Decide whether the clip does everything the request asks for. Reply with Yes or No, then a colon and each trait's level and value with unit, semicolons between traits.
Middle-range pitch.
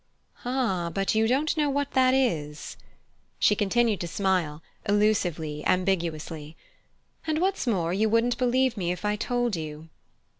No: high, 205 Hz